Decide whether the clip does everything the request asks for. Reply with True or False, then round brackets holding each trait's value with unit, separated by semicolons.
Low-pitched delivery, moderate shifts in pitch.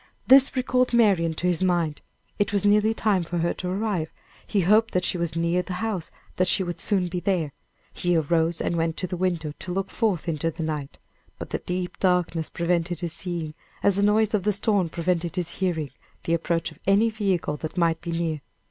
False (180 Hz; 3.2 semitones)